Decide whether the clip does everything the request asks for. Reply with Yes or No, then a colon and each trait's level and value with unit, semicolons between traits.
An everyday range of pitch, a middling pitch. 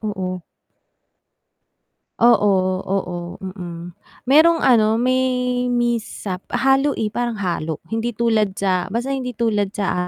No: average, 4.2 semitones; high, 215 Hz